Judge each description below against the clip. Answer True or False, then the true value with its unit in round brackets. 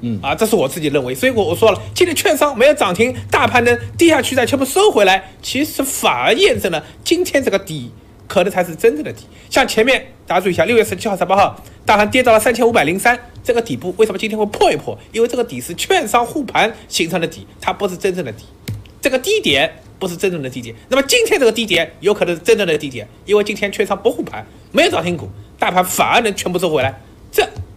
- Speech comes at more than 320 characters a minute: True (370 characters per minute)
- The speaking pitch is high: True (205 Hz)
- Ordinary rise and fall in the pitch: False (6.8 semitones)